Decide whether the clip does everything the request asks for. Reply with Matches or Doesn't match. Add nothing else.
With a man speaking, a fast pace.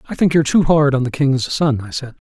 Matches